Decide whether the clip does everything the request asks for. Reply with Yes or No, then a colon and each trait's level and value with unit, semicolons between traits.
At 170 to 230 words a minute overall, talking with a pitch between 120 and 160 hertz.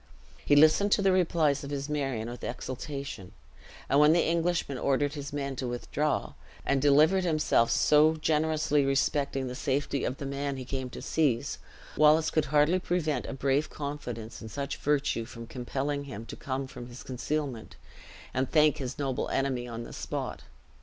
Yes: average, 175 wpm; medium, 140 Hz